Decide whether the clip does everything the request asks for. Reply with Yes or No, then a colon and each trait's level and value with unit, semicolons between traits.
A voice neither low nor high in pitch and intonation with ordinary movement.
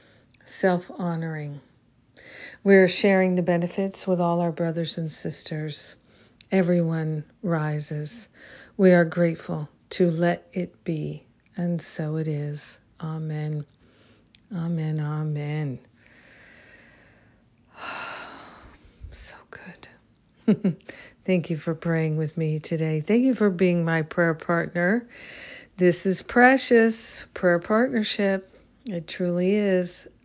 Yes: medium, 170 Hz; average, 3.5 semitones